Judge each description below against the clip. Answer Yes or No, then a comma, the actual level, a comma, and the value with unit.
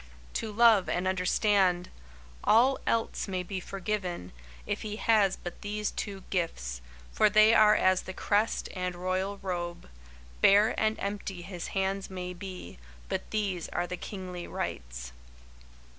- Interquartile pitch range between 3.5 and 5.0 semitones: No, average, 2.7 semitones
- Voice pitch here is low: No, high, 190 Hz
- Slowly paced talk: No, average, 145 wpm